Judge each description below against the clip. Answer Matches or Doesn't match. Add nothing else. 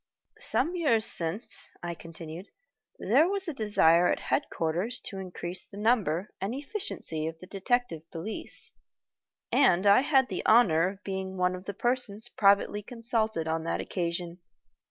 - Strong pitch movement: Matches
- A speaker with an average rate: Matches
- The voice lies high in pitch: Matches